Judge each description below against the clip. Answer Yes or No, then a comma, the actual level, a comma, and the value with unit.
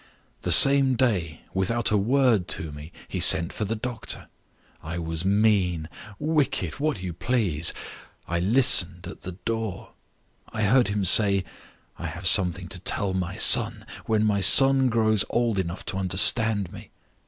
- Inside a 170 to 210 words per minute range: No, average, 155 wpm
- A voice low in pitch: Yes, low, 100 Hz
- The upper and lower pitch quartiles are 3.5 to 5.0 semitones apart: Yes, average, 4.5 semitones